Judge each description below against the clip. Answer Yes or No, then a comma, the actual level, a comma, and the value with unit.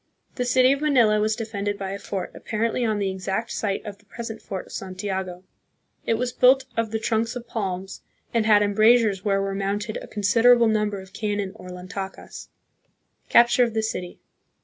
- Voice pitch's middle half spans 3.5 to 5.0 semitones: No, average, 2.8 semitones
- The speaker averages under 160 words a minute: No, average, 185 wpm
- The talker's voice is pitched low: No, high, 210 Hz